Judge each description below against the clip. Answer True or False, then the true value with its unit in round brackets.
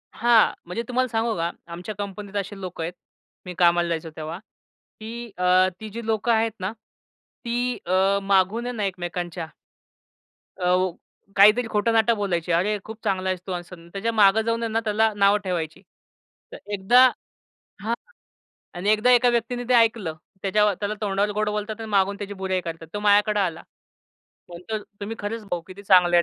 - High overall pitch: True (205 Hz)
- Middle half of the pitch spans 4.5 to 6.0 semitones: False (3.5 semitones)